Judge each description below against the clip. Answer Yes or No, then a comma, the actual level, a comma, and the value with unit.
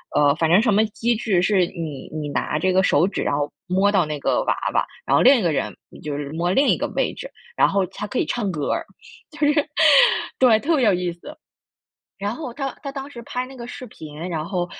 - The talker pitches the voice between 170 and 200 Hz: Yes, high, 195 Hz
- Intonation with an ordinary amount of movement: No, wide, 6.8 semitones